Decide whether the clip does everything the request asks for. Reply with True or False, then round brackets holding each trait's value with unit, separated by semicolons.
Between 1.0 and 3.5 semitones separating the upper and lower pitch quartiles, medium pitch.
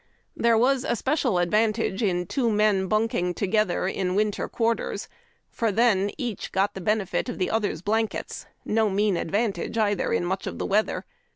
False (2.9 semitones; 210 Hz)